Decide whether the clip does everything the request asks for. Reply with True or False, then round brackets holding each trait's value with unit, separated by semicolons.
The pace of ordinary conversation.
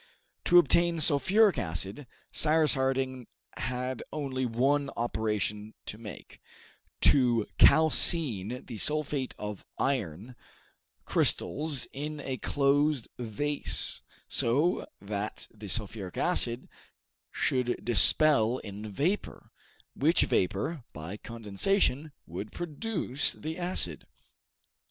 False (95 wpm)